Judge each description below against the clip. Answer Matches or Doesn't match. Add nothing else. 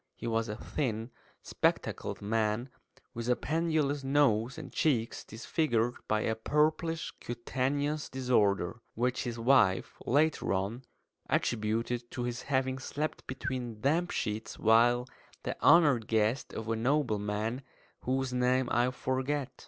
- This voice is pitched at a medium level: Doesn't match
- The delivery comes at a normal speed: Doesn't match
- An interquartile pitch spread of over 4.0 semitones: Doesn't match